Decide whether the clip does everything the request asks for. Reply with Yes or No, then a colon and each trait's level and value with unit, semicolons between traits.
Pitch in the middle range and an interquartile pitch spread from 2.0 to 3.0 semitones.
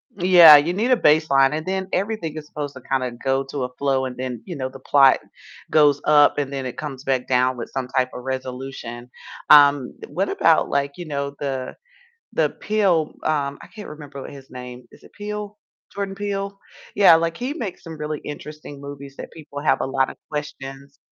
No: medium, 145 Hz; average, 3.7 semitones